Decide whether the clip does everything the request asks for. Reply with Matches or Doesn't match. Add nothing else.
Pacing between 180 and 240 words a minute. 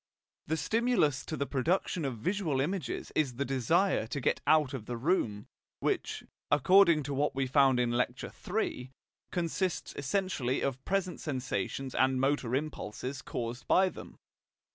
Doesn't match